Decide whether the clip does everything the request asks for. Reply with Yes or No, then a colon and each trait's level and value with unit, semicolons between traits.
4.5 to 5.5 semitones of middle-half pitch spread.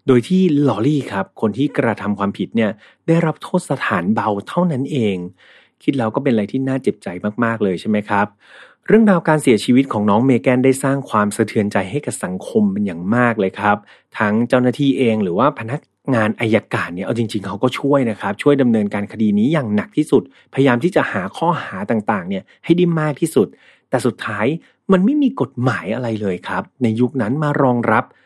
Yes: average, 5.2 semitones